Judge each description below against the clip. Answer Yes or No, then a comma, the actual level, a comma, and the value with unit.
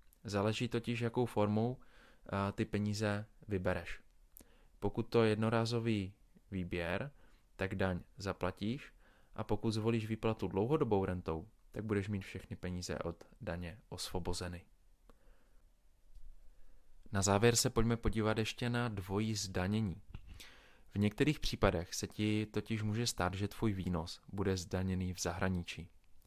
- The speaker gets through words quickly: No, average, 120 wpm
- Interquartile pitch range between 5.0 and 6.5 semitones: No, average, 3.4 semitones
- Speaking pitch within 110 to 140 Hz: No, low, 100 Hz